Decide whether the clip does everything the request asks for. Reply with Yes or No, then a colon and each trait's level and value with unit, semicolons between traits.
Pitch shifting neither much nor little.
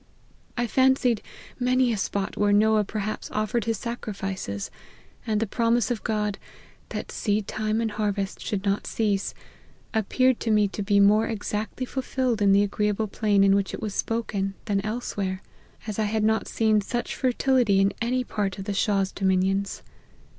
No: narrow, 2.3 semitones